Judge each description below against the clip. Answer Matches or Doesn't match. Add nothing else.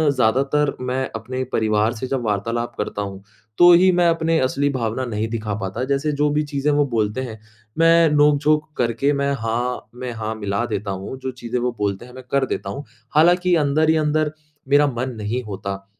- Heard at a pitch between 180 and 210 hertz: Doesn't match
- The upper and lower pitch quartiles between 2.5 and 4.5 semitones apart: Doesn't match